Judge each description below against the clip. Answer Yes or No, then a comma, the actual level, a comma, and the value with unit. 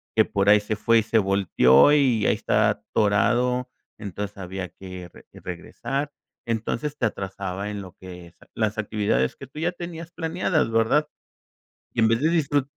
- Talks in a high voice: No, low, 110 Hz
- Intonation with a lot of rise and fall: Yes, wide, 6.0 semitones